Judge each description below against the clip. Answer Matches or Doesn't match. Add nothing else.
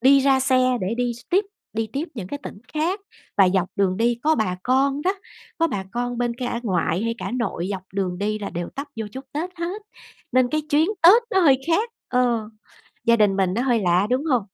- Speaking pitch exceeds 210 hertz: Matches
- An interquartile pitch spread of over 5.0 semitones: Matches